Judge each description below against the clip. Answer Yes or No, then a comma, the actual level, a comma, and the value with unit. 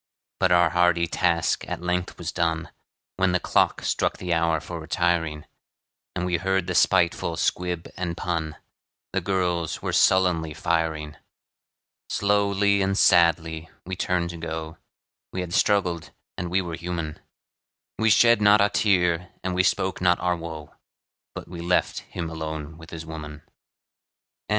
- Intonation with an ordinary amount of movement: No, narrow, 2.0 semitones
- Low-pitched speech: Yes, very low, 85 Hz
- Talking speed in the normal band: Yes, average, 150 wpm